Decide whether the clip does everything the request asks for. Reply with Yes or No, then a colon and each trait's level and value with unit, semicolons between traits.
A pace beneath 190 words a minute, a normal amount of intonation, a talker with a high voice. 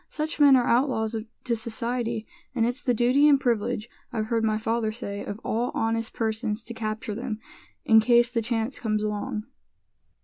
No: average, 175 wpm; narrow, 2.1 semitones; high, 230 Hz